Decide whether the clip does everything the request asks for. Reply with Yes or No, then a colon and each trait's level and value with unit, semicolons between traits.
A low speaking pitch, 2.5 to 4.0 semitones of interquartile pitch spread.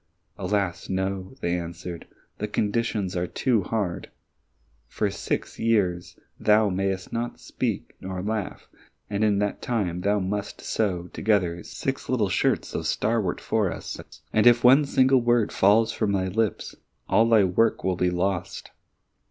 Yes: low, 100 Hz; average, 3.4 semitones